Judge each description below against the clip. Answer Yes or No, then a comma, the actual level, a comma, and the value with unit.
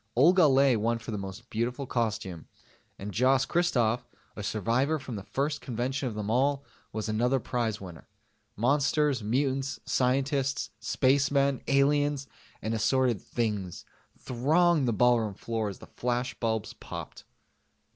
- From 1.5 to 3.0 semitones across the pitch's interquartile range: No, average, 3.8 semitones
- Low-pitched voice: Yes, low, 125 Hz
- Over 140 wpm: No, slow, 135 wpm